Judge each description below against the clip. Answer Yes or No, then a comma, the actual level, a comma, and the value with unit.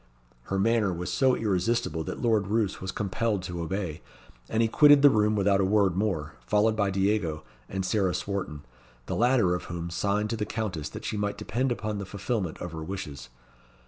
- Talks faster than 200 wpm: No, average, 195 wpm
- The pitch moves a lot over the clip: No, average, 3.3 semitones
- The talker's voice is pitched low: Yes, low, 100 Hz